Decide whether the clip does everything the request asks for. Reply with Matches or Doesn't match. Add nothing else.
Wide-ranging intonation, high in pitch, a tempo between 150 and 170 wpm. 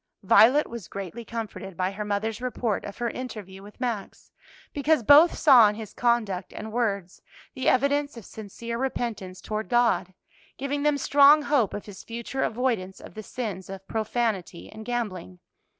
Doesn't match